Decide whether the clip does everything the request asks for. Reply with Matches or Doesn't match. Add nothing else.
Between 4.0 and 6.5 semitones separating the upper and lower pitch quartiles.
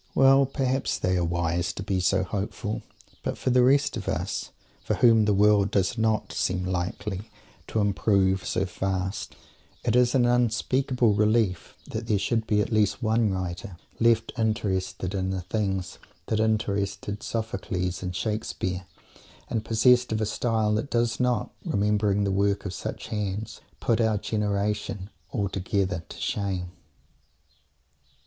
Doesn't match